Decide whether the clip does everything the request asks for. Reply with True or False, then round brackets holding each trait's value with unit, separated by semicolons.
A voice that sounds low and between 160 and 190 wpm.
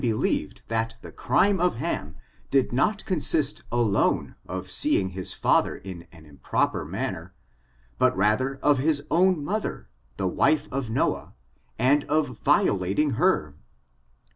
False (130 Hz; 140 wpm)